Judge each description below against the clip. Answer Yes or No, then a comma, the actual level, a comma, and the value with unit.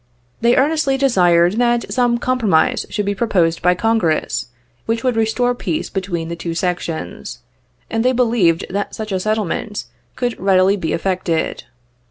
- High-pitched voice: Yes, high, 210 Hz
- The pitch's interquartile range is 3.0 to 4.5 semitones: No, average, 5.2 semitones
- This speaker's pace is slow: No, average, 150 wpm